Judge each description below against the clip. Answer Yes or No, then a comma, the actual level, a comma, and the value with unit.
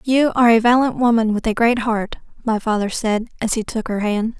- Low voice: No, high, 225 Hz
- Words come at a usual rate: No, fast, 230 wpm